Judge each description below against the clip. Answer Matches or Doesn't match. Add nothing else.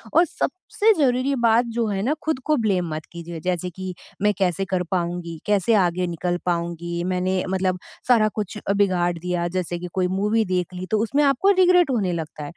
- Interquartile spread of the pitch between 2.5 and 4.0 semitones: Doesn't match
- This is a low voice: Doesn't match